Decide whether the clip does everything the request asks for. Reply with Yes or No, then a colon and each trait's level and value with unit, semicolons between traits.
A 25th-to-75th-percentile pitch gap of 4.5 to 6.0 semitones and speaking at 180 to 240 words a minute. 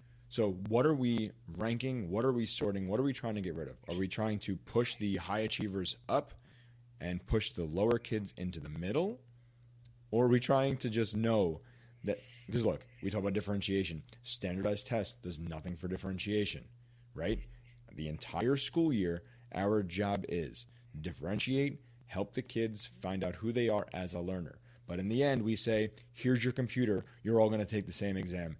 No: average, 3.8 semitones; average, 190 wpm